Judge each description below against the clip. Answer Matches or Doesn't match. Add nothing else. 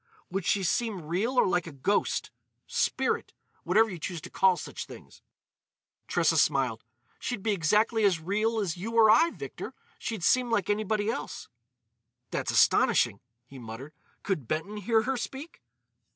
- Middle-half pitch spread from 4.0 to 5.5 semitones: Matches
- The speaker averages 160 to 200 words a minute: Doesn't match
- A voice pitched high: Matches